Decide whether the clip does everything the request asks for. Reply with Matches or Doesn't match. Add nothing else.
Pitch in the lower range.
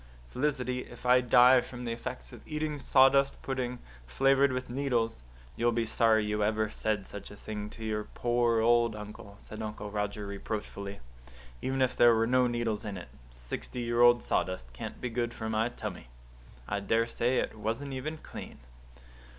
Matches